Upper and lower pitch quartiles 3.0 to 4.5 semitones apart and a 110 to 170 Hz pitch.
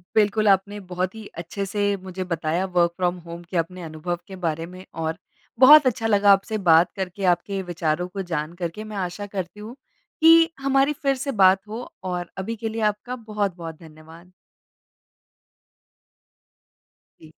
No: average, 3.6 semitones; high, 190 Hz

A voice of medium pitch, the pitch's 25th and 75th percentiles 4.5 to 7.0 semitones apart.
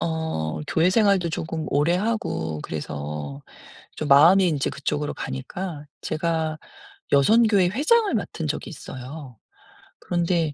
Yes: medium, 160 Hz; average, 5.0 semitones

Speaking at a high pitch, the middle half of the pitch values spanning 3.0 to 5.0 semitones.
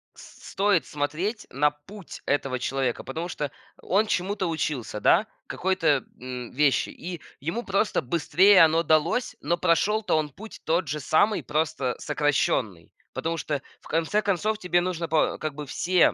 No: medium, 160 Hz; average, 4.5 semitones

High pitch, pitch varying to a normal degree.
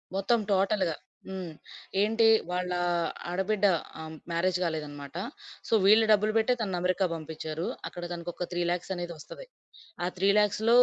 No: medium, 180 Hz; average, 3.4 semitones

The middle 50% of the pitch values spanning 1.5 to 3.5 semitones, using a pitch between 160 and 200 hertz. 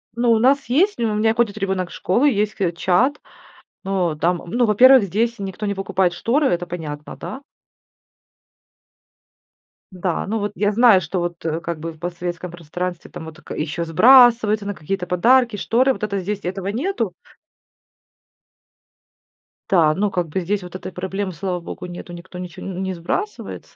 No: average, 4.3 semitones; high, 190 Hz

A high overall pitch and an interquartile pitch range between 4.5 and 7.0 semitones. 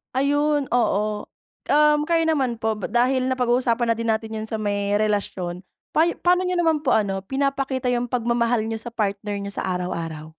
Yes: high, 235 Hz; average, 4.8 semitones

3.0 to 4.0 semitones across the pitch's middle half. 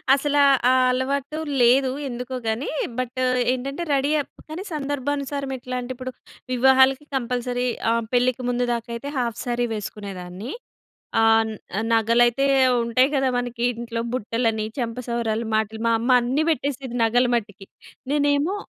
No: narrow, 2.6 semitones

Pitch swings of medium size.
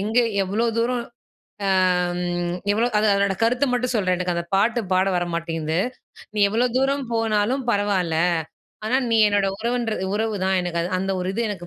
Yes: average, 4.1 semitones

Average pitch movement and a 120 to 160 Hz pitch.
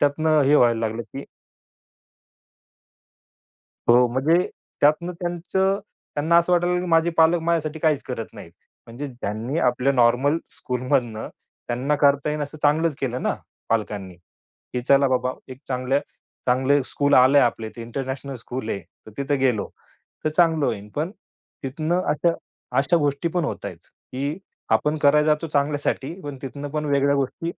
Yes: average, 3.6 semitones; medium, 140 Hz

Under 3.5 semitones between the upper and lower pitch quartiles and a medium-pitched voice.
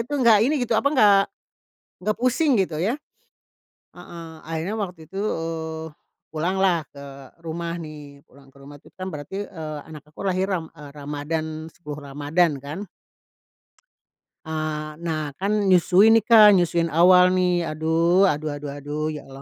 No: average, 3.8 semitones; medium, 165 Hz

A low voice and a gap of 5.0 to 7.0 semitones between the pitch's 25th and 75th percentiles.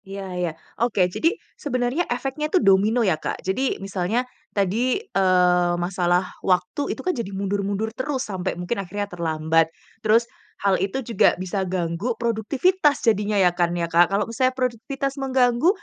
No: high, 205 Hz; wide, 5.6 semitones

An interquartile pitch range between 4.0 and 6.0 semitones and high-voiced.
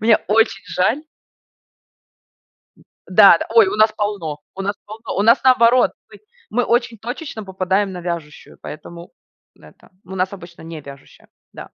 Yes: average, 4.8 semitones; high, 200 Hz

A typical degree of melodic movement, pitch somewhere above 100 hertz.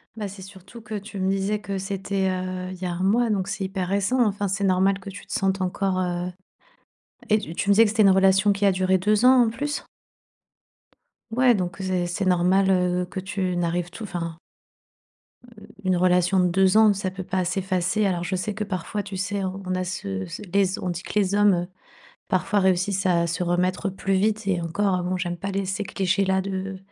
No: narrow, 1.7 semitones; high, 190 Hz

